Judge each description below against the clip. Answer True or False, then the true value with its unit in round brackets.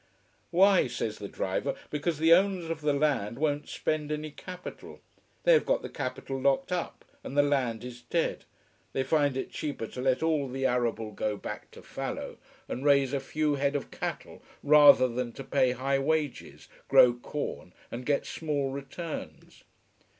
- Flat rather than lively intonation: False (3.3 semitones)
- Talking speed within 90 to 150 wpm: False (170 wpm)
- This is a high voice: False (140 Hz)